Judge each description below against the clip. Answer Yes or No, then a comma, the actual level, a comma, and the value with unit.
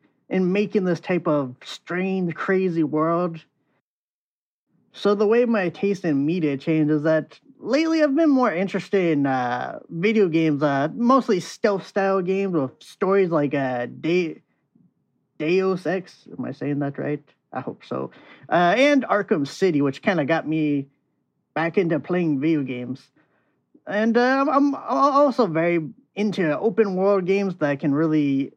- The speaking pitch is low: No, medium, 175 Hz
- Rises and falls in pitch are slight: No, average, 5.1 semitones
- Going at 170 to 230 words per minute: No, average, 155 wpm